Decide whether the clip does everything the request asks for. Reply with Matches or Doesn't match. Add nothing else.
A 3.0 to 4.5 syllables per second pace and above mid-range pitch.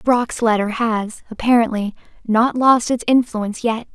Matches